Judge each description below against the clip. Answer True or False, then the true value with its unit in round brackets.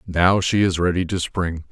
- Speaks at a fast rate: True (210 wpm)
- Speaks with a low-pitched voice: True (90 Hz)